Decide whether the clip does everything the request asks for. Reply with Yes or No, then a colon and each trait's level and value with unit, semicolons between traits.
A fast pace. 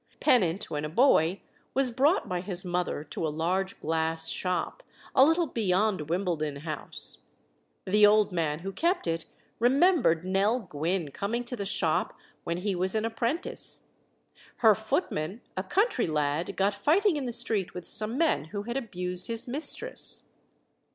No: average, 160 wpm